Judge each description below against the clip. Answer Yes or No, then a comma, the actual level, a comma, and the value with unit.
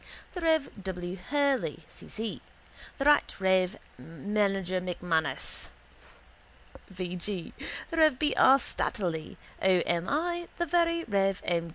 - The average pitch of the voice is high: Yes, high, 195 Hz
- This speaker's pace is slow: Yes, slow, 130 wpm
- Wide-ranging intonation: Yes, wide, 8.6 semitones